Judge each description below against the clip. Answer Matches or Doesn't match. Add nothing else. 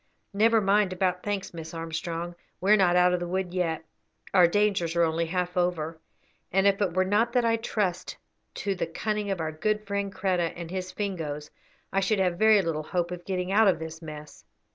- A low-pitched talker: Doesn't match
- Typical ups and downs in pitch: Matches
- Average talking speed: Doesn't match